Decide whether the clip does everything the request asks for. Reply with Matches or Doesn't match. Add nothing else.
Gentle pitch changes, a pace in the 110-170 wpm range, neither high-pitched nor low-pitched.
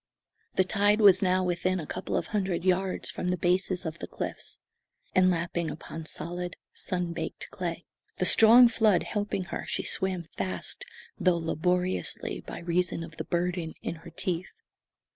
Matches